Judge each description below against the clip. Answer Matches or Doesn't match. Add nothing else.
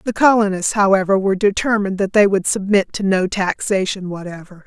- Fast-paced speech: Doesn't match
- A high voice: Matches